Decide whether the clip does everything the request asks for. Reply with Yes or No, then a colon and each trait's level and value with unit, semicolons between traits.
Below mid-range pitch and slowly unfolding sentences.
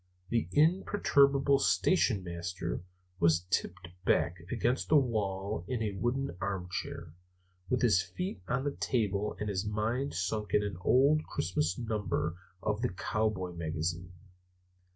Yes: low, 105 Hz; slow, 130 wpm